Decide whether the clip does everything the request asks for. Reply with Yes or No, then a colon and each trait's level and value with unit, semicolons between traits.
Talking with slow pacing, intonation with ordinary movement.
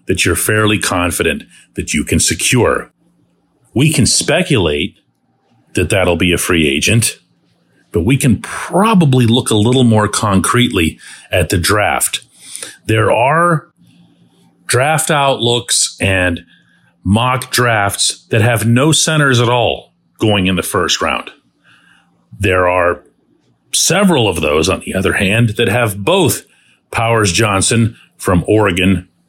Yes: slow, 130 wpm; average, 4.5 semitones